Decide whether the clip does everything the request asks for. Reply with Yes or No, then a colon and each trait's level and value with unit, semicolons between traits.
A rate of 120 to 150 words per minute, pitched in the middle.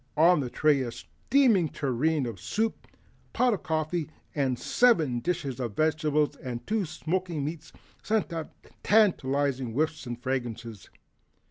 Yes: average, 140 wpm; medium, 155 Hz